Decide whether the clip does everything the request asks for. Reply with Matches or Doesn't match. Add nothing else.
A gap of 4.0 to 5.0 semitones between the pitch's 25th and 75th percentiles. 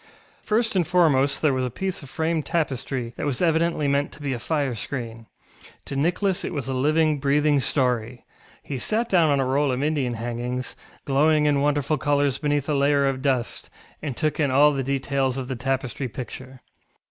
Doesn't match